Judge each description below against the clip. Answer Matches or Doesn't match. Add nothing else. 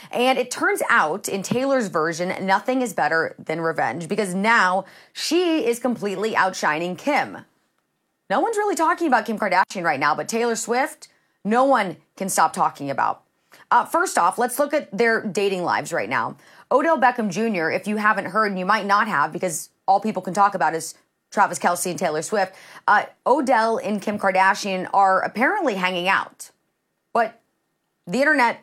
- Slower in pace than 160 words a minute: Doesn't match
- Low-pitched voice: Doesn't match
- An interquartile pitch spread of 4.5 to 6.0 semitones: Matches